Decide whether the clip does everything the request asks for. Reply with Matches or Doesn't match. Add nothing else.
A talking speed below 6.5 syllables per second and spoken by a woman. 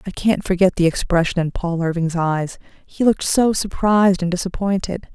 Matches